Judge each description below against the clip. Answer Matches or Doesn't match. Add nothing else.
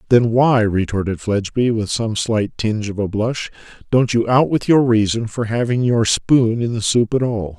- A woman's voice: Doesn't match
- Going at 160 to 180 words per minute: Doesn't match